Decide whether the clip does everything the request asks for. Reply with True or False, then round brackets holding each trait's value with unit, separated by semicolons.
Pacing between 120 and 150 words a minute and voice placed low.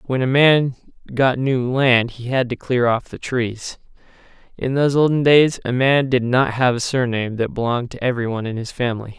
False (200 wpm; 125 Hz)